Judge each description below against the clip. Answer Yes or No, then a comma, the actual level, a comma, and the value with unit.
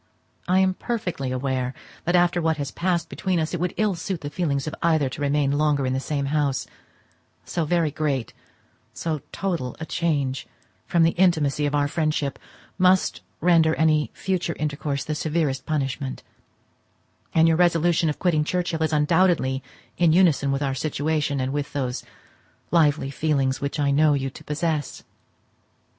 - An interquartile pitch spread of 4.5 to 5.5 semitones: No, average, 3.3 semitones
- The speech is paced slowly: No, average, 160 wpm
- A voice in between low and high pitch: Yes, medium, 155 Hz